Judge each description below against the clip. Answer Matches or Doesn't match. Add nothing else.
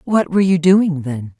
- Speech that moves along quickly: Matches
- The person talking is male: Doesn't match